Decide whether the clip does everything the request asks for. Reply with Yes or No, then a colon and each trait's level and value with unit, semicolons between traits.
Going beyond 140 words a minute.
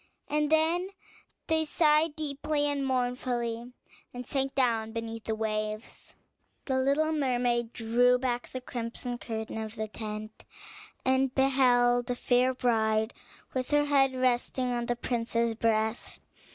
No: slow, 135 wpm